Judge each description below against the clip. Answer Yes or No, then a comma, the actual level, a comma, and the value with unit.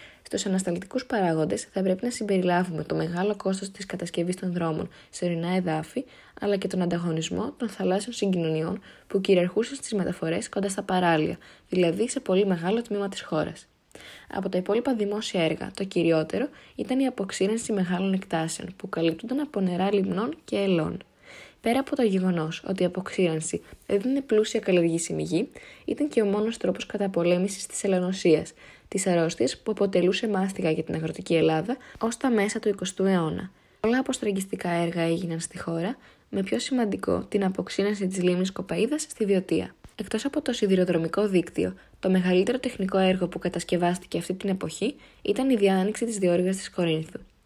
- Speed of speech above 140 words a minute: Yes, average, 160 wpm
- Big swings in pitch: No, average, 3.4 semitones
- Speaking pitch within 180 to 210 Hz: Yes, high, 190 Hz